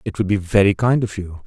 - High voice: No, low, 100 Hz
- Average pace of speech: No, fast, 285 wpm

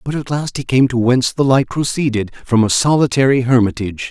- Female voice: No, male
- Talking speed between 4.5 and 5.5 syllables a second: No, 5.9 syllables/s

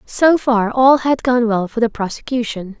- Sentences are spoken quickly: No, average, 195 wpm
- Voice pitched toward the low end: No, high, 235 Hz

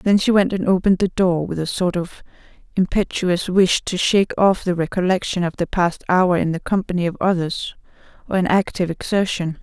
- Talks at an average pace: Yes, average, 195 wpm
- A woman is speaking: Yes, female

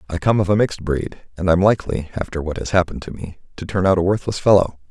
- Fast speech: Yes, fast, 255 wpm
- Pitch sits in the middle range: No, very low, 90 Hz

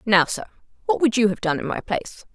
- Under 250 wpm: No, fast, 255 wpm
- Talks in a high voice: Yes, high, 200 Hz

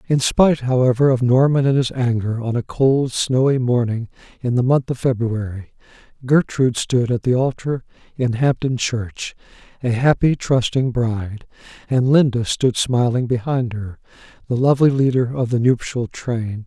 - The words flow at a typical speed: Yes, average, 155 wpm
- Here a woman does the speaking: No, male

